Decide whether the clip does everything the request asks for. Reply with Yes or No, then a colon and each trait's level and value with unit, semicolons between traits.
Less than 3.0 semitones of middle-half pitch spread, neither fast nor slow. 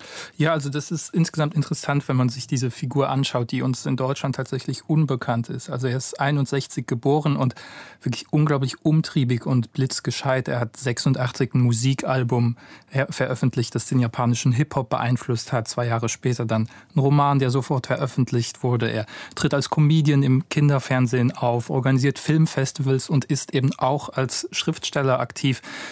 Yes: narrow, 2.4 semitones; average, 155 wpm